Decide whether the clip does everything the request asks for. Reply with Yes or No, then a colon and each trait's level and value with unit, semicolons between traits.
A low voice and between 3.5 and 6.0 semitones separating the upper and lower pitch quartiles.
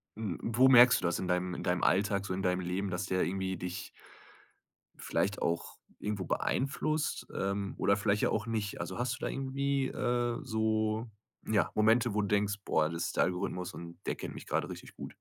Yes: low, 100 Hz; average, 3.9 semitones